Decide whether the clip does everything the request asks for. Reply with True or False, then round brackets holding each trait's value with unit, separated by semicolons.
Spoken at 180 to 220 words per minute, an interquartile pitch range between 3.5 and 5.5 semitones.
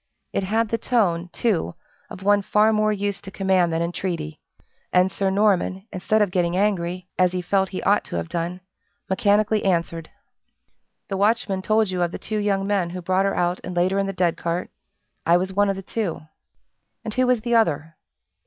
False (200 wpm; 2.7 semitones)